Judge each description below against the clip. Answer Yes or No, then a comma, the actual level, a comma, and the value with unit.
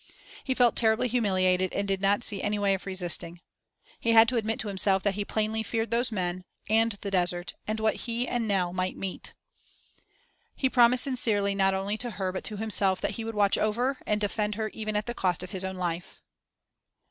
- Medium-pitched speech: No, high, 210 Hz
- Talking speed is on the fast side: Yes, fast, 210 wpm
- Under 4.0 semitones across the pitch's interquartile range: Yes, average, 3.0 semitones